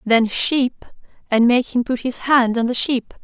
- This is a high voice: Yes, high, 245 Hz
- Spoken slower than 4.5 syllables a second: Yes, 4.0 syllables/s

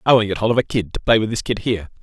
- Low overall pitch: Yes, low, 110 Hz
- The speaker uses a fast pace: Yes, fast, 415 wpm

